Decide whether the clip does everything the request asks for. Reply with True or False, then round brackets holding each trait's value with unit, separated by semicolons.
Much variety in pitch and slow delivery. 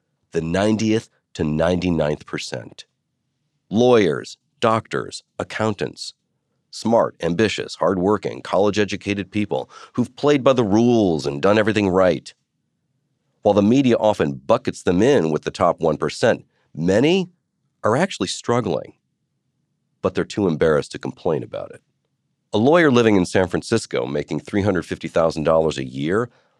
True (7.2 semitones; 125 wpm)